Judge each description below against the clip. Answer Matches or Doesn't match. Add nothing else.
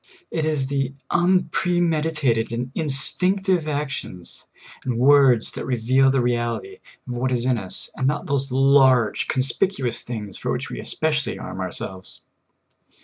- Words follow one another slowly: Doesn't match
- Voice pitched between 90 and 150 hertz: Matches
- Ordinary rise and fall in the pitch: Matches